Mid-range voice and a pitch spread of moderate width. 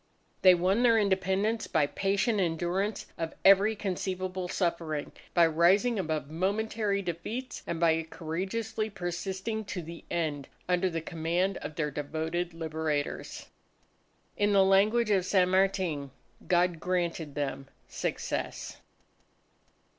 Yes: medium, 180 Hz; average, 3.3 semitones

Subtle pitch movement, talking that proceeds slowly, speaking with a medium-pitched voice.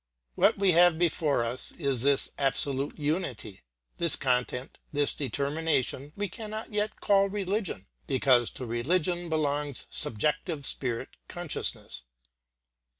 No: average, 5.1 semitones; slow, 115 wpm; medium, 145 Hz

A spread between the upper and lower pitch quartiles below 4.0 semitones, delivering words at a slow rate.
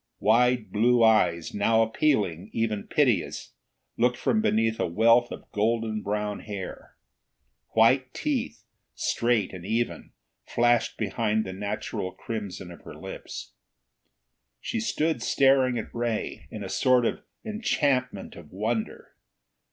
Yes: average, 2.9 semitones; slow, 125 wpm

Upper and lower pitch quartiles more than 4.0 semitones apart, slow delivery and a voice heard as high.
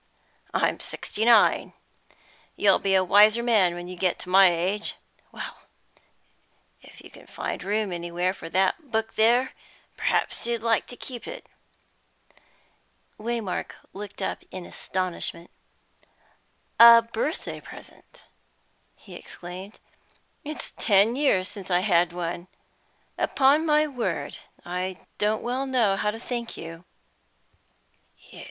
Yes: average, 4.5 semitones; slow, 125 wpm; high, 205 Hz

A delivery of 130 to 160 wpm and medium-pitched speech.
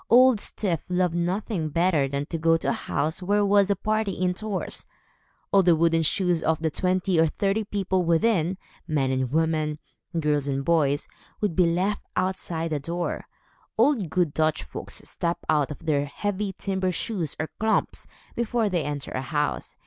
No: average, 170 wpm; medium, 170 Hz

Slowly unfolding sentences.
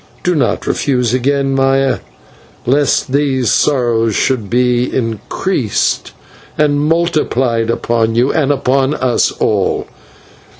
Yes: slow, 115 wpm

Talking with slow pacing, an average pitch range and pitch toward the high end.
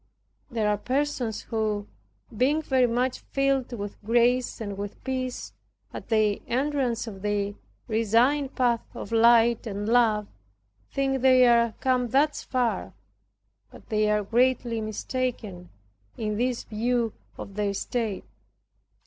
Yes: slow, 130 wpm; average, 3.3 semitones; high, 235 Hz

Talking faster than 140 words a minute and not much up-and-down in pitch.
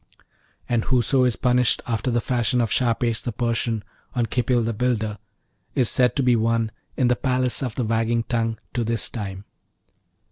Yes: average, 175 wpm; narrow, 1.7 semitones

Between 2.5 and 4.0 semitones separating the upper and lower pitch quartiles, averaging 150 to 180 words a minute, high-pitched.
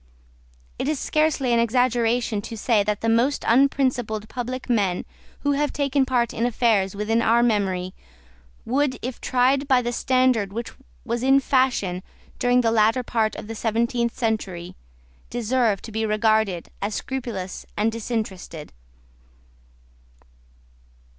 No: average, 3.0 semitones; slow, 135 wpm; high, 235 Hz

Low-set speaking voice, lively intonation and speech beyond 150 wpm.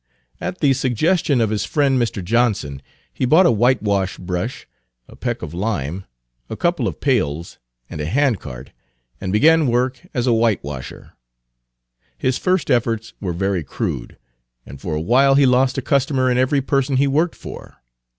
Yes: low, 120 Hz; wide, 6.2 semitones; average, 165 wpm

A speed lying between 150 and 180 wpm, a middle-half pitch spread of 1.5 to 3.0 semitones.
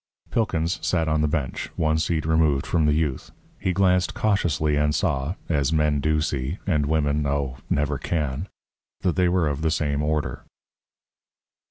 Yes: average, 165 wpm; narrow, 2.5 semitones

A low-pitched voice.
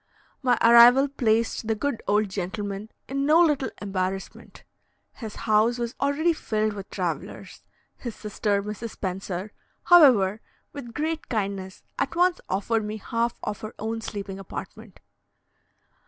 No: high, 220 Hz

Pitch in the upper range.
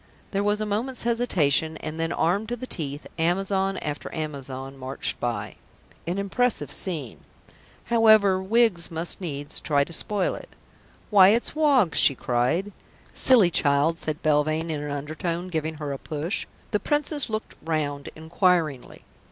No: medium, 165 Hz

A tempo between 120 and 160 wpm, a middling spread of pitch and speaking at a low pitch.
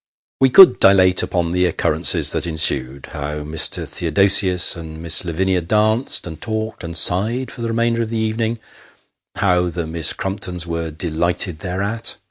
Yes: average, 155 wpm; average, 4.8 semitones; very low, 90 Hz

